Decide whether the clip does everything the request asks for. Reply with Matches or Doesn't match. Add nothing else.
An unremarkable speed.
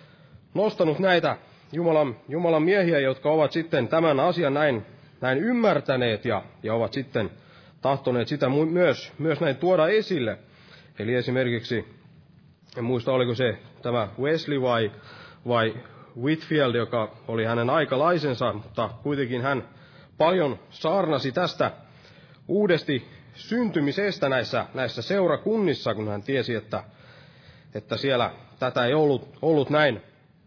Matches